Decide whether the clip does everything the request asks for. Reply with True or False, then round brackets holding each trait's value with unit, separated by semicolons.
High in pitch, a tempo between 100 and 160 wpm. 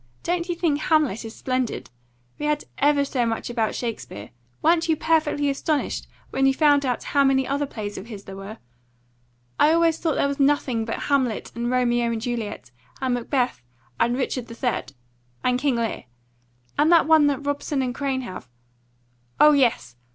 False (265 Hz; 175 wpm)